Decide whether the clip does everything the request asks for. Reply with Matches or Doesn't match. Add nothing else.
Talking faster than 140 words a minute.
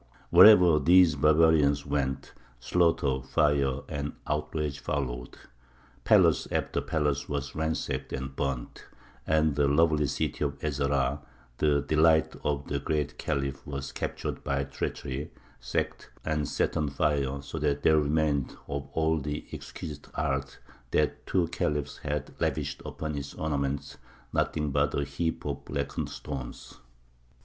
Doesn't match